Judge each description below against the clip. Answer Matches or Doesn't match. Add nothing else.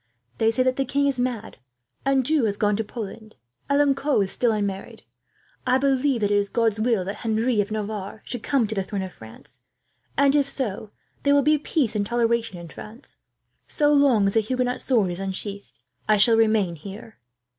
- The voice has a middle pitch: Doesn't match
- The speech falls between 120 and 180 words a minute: Doesn't match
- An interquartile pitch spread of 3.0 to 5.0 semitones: Matches